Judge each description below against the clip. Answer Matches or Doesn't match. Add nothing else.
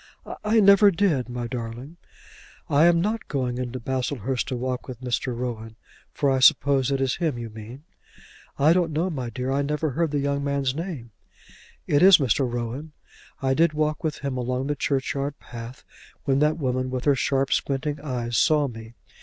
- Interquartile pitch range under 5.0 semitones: Matches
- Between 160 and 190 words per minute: Matches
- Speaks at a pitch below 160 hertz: Matches